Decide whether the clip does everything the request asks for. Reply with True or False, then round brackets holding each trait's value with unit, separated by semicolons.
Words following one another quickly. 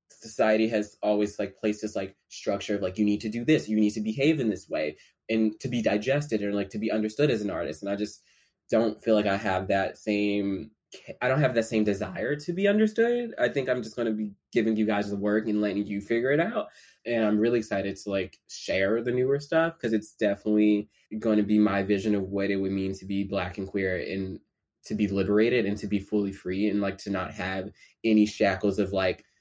True (240 wpm)